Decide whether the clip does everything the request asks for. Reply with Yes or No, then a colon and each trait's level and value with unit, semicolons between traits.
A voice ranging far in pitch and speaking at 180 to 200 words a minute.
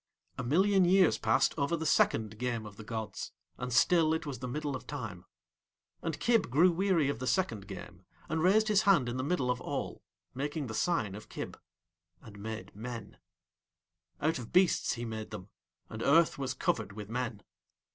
Yes: wide, 6.7 semitones; average, 185 wpm